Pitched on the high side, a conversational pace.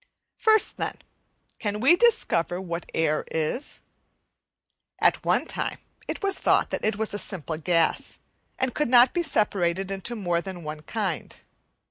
Yes: high, 195 Hz; average, 150 wpm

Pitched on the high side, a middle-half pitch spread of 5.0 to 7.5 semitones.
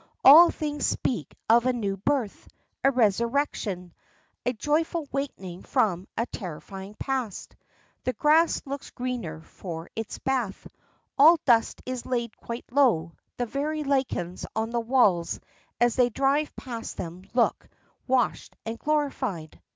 Yes: high, 240 Hz; wide, 5.6 semitones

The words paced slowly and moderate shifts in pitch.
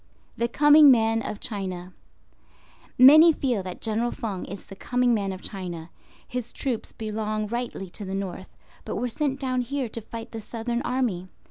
No: average, 170 wpm; average, 4.2 semitones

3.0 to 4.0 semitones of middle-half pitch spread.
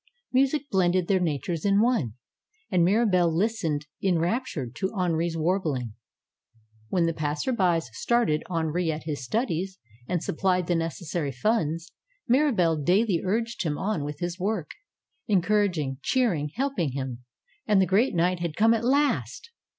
No: average, 5.1 semitones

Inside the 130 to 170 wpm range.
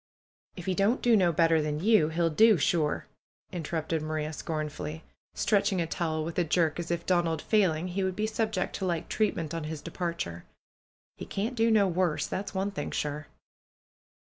No: average, 185 wpm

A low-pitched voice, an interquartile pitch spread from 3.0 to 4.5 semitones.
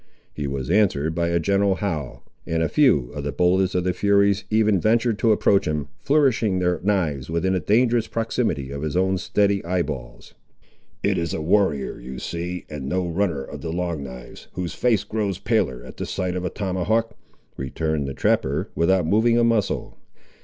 No: very low, 90 Hz; average, 4.9 semitones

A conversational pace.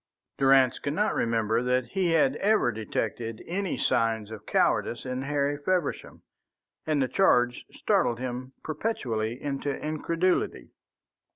No: slow, 125 wpm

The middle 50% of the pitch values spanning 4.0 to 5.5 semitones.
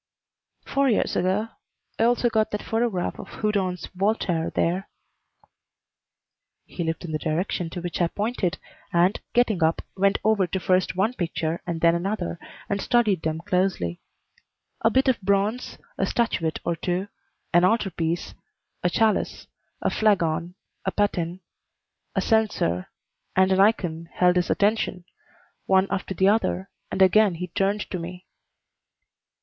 No: average, 3.5 semitones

